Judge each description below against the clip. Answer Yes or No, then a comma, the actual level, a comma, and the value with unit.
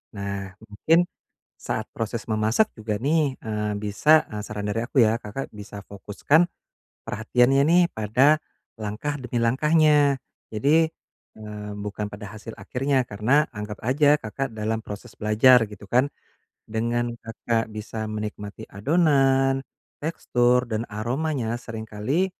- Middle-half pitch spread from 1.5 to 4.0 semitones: No, average, 4.4 semitones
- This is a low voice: Yes, low, 115 Hz